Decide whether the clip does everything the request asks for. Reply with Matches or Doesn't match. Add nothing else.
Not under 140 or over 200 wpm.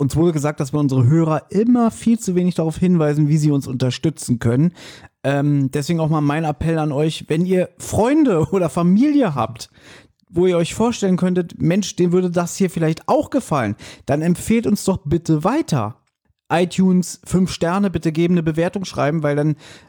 Matches